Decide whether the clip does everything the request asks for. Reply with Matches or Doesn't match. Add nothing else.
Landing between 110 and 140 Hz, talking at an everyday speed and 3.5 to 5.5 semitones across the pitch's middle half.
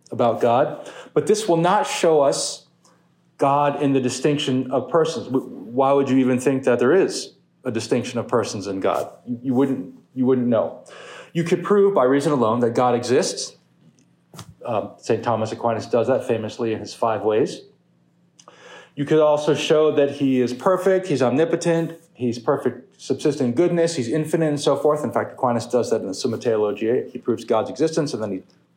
Matches